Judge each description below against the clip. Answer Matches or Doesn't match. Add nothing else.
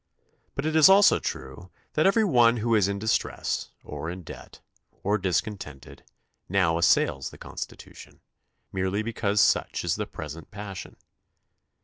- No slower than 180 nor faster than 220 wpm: Doesn't match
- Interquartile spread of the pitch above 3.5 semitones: Matches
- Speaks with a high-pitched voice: Doesn't match